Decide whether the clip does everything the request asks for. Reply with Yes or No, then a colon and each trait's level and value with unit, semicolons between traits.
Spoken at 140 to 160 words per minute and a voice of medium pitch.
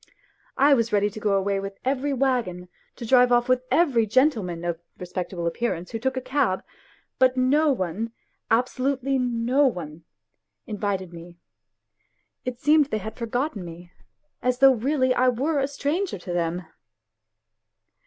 No: average, 155 wpm; high, 240 Hz